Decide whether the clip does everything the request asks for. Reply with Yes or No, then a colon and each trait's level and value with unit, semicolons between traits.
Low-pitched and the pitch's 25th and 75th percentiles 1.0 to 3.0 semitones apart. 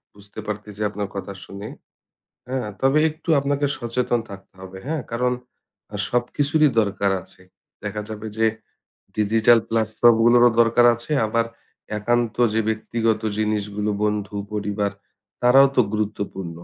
Yes: low, 110 Hz; average, 2.7 semitones